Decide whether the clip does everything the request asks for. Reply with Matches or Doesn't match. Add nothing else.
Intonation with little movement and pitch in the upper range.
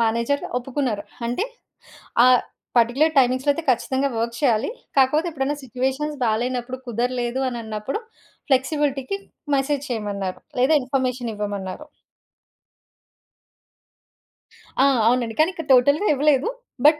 Doesn't match